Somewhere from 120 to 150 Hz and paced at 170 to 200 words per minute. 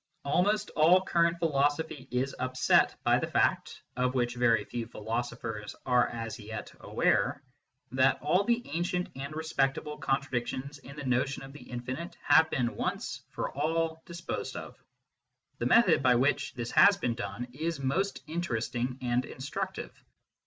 No: low, 135 Hz; average, 155 wpm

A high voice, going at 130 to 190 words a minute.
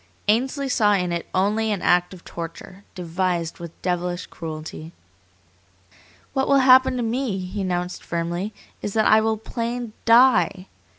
Yes: high, 195 Hz; average, 145 wpm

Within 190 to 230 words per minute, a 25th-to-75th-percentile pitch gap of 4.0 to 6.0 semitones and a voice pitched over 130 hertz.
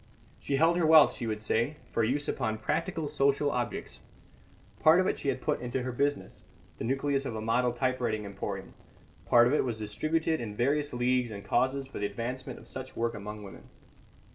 No: average, 195 wpm; average, 4.3 semitones; low, 125 Hz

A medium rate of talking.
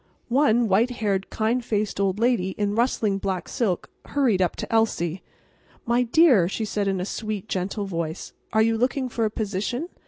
Yes: average, 180 wpm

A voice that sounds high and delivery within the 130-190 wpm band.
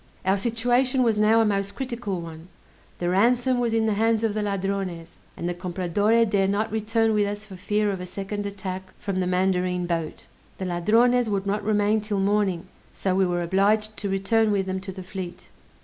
No: high, 200 Hz; average, 200 wpm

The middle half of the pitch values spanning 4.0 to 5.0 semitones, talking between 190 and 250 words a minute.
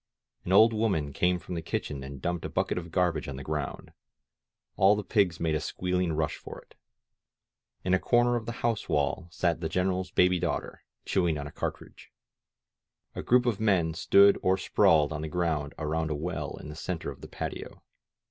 No: average, 3.5 semitones; average, 195 wpm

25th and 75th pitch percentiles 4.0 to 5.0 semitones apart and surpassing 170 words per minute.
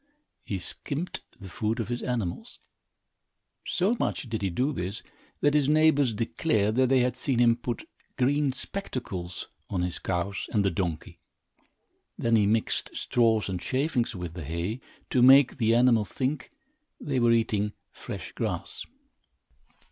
No: average, 4.7 semitones; average, 150 wpm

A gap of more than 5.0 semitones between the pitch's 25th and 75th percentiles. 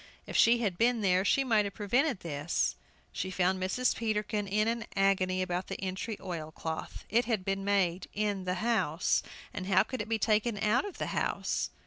No: average, 3.3 semitones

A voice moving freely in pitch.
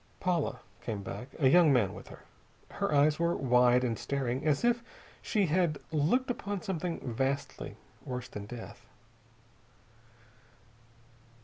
Yes: wide, 5.8 semitones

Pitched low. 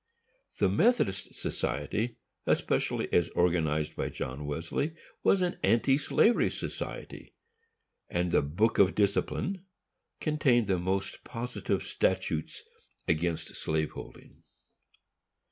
Yes: very low, 95 Hz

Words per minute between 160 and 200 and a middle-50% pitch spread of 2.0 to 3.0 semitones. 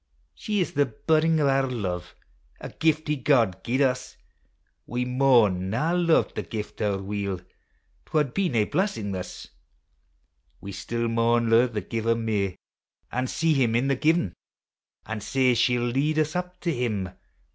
No: average, 165 wpm; wide, 5.5 semitones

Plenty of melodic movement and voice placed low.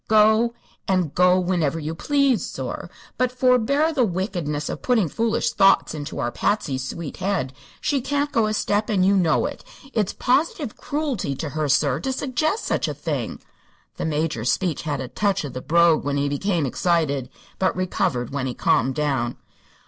No: wide, 7.9 semitones; medium, 180 Hz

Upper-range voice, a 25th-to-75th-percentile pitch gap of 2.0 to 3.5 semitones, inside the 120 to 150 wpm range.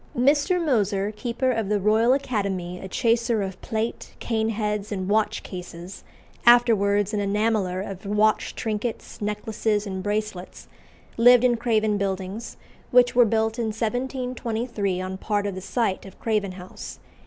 Yes: high, 215 Hz; average, 2.8 semitones; average, 145 wpm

